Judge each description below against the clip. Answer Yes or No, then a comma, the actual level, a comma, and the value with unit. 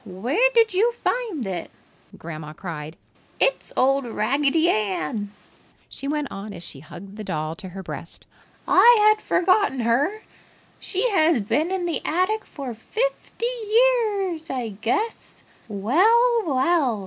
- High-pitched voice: Yes, very high, 285 Hz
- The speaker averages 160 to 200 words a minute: No, slow, 135 wpm